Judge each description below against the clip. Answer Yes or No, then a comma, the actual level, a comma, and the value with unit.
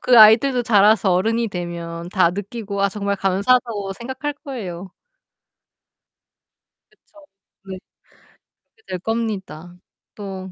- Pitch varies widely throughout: No, average, 3.7 semitones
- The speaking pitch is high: Yes, high, 200 Hz